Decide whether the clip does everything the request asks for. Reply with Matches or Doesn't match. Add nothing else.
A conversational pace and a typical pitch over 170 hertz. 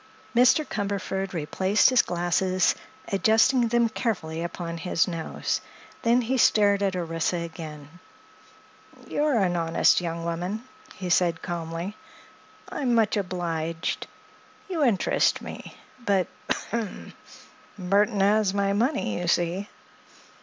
Doesn't match